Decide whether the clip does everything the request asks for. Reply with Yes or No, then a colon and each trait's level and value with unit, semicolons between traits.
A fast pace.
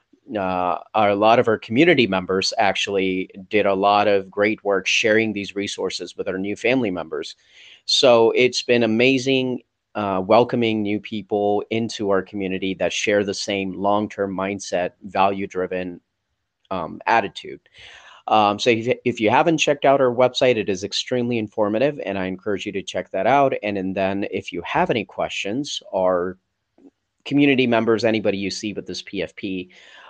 No: average, 165 wpm